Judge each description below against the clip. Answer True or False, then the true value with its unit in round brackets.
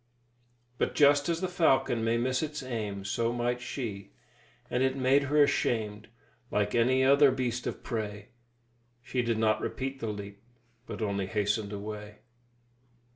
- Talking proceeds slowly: False (150 wpm)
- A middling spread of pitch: True (4.0 semitones)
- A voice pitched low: True (120 Hz)